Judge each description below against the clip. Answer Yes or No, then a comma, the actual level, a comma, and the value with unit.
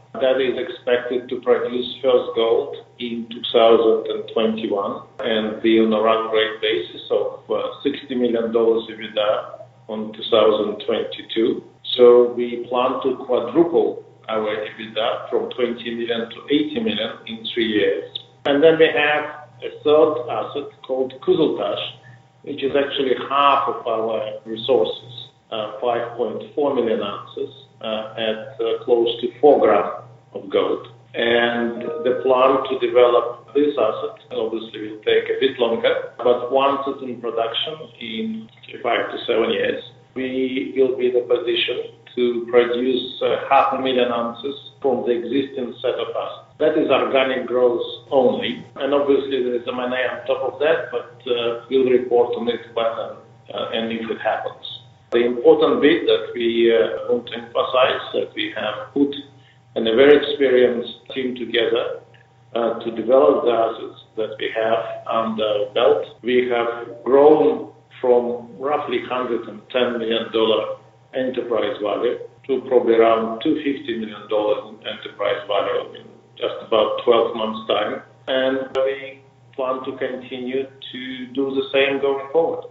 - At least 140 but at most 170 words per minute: Yes, average, 145 wpm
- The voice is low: Yes, low, 130 Hz